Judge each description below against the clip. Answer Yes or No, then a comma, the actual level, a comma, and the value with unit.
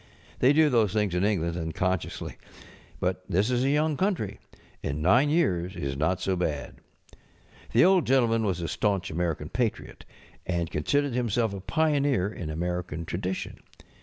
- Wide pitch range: Yes, wide, 6.5 semitones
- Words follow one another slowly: No, average, 160 wpm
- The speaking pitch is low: Yes, very low, 95 Hz